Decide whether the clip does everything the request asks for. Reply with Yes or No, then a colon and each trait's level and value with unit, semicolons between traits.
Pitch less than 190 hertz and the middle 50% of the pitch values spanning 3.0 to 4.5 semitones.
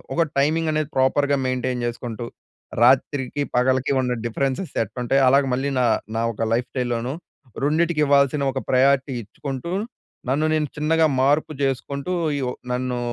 No: low, 135 Hz; narrow, 2.5 semitones